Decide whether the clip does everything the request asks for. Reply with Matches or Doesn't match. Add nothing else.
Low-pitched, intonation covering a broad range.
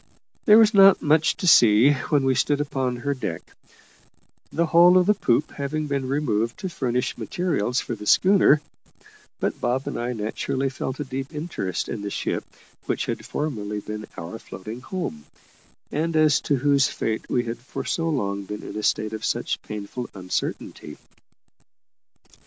Matches